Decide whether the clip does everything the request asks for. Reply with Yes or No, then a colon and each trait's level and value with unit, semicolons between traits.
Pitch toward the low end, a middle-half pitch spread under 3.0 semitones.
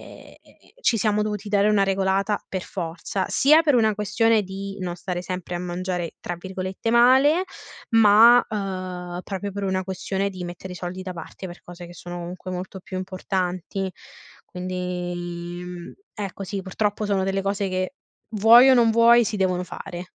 No: high, 190 Hz; narrow, 2.5 semitones